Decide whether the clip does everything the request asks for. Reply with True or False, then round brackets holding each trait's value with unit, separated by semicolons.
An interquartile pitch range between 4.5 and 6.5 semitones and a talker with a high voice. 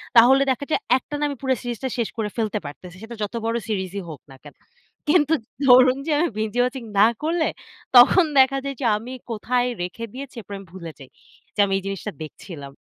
True (5.1 semitones; 235 Hz)